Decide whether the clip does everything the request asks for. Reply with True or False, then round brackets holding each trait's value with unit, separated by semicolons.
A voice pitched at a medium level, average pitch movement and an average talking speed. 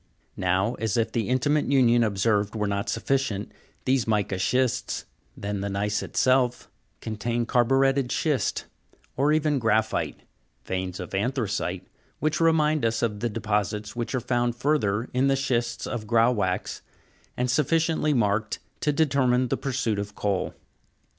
False (120 Hz; 4.2 semitones; 145 wpm)